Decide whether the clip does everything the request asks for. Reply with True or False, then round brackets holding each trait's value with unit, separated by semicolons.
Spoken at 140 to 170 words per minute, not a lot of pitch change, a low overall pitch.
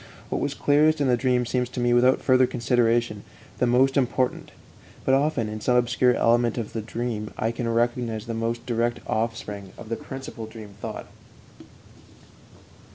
True (165 wpm; 1.7 semitones; 120 Hz)